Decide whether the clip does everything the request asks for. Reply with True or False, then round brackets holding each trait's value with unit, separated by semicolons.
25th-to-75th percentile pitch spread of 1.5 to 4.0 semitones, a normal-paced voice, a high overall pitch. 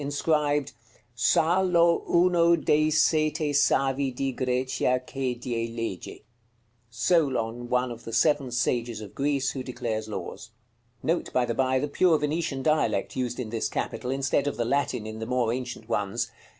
False (3.7 semitones; 155 wpm; 130 Hz)